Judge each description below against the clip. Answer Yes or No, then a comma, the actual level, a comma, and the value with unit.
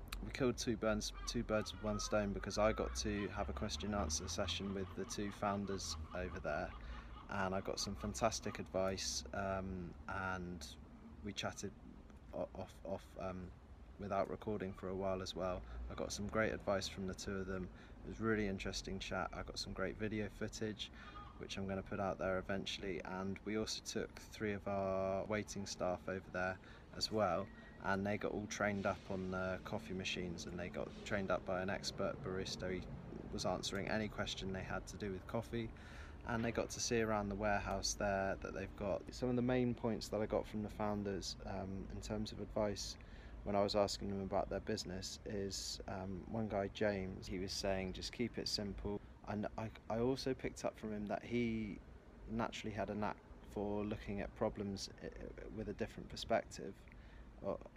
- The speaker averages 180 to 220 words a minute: Yes, average, 195 wpm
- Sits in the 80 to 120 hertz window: Yes, low, 100 Hz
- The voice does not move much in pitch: Yes, narrow, 2.1 semitones